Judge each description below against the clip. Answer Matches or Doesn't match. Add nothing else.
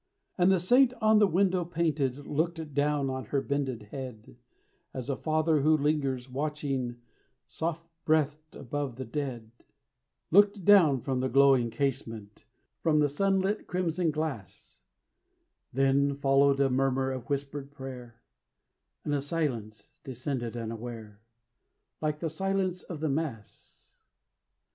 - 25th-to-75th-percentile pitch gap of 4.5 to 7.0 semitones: Doesn't match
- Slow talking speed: Matches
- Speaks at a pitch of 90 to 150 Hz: Matches